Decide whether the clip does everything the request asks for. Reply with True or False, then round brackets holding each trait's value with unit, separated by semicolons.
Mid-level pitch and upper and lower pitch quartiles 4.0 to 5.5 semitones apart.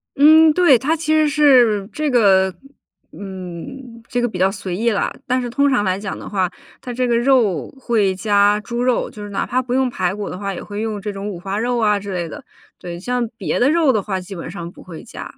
False (215 Hz; 4.7 semitones)